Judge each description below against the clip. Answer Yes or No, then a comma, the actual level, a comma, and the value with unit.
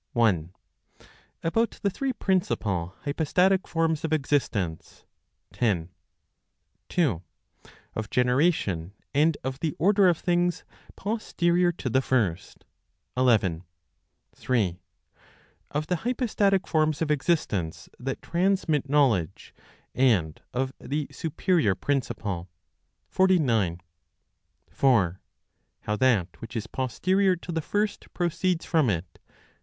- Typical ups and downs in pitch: No, wide, 8.6 semitones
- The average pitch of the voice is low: No, medium, 145 Hz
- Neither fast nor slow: No, slow, 105 wpm